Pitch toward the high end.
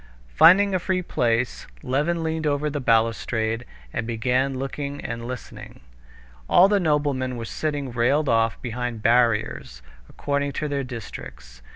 No: low, 130 Hz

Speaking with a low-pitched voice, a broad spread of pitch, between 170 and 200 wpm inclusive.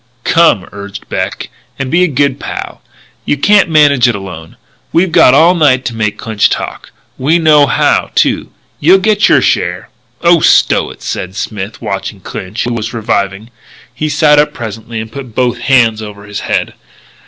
Yes: low, 120 Hz; wide, 6.2 semitones; average, 175 wpm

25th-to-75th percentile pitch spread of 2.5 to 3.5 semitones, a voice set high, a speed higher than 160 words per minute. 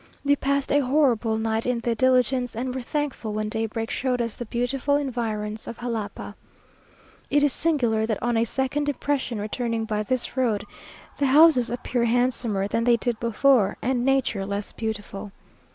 Yes: average, 3.0 semitones; high, 240 Hz; average, 170 wpm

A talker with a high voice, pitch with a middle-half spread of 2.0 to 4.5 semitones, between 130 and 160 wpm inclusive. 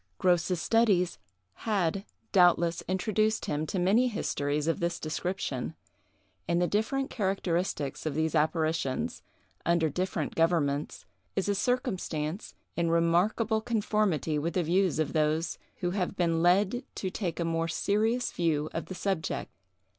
No: medium, 175 Hz; average, 3.8 semitones; average, 140 wpm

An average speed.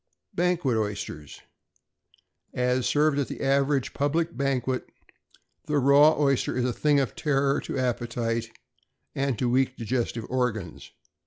No: slow, 130 wpm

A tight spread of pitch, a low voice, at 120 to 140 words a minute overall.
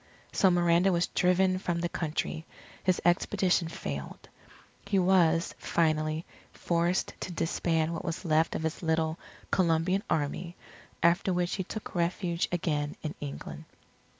No: narrow, 2.1 semitones; medium, 170 Hz; slow, 135 wpm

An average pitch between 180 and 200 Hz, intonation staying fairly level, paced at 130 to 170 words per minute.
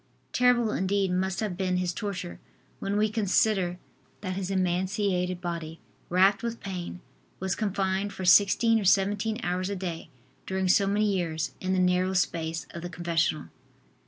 Yes: high, 190 Hz; narrow, 2.1 semitones; average, 160 wpm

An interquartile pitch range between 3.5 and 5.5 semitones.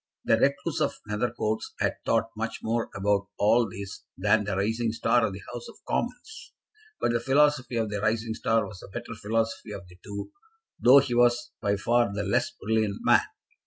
No: average, 2.8 semitones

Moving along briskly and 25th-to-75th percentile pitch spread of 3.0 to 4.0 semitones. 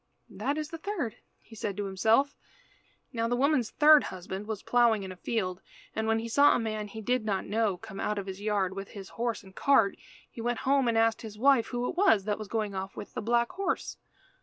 Yes: fast, 235 wpm; average, 3.4 semitones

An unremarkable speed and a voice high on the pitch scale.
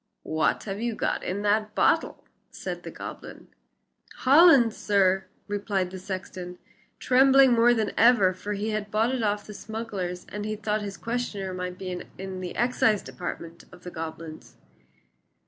Yes: average, 160 wpm; high, 205 Hz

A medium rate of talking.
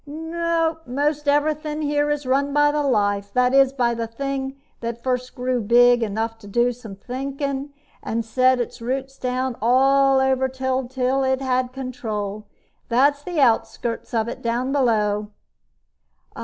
Yes: average, 150 wpm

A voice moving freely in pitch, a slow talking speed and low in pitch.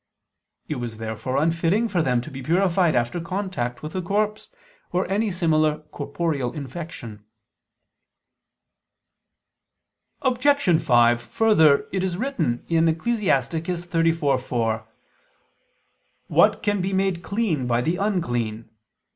No: wide, 6.9 semitones; slow, 110 wpm; medium, 165 Hz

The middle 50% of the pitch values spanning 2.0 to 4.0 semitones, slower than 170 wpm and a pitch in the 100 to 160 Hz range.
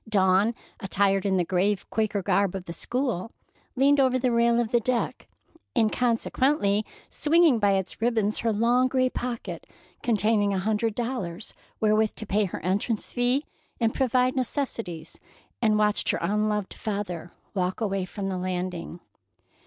No: average, 3.7 semitones; average, 150 wpm; high, 215 Hz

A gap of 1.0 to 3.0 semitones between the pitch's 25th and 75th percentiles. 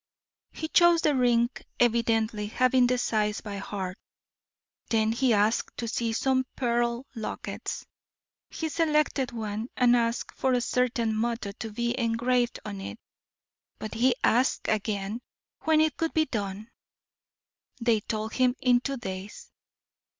Yes: average, 2.7 semitones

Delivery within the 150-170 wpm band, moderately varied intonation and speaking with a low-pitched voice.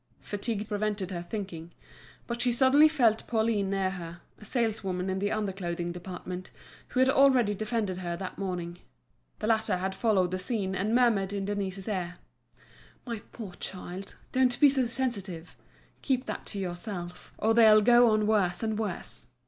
No: average, 165 wpm; average, 3.7 semitones; high, 205 Hz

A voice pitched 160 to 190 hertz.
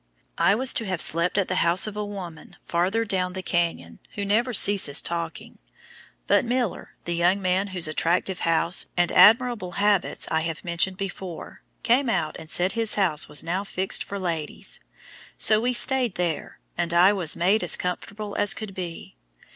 Yes: medium, 185 Hz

